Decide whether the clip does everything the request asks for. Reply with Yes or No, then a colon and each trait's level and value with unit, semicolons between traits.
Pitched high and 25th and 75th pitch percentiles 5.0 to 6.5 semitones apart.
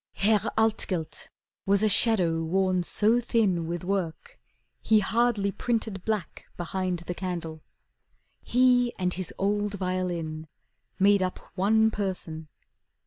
No: high, 195 Hz; average, 3.6 semitones